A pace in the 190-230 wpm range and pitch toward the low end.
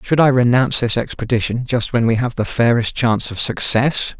Yes: average, 200 wpm; low, 120 Hz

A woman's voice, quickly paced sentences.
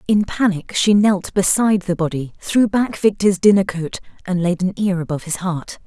No: female; average, 195 wpm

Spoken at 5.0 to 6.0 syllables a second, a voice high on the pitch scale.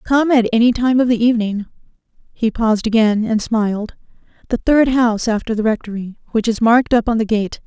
Yes: 5.9 syllables/s; high, 225 Hz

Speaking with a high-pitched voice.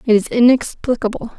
Yes: high, 235 Hz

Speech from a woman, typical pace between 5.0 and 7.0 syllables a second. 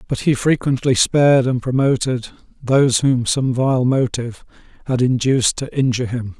No: male; 5.1 syllables/s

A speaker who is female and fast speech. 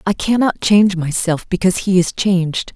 No: female; average, 175 wpm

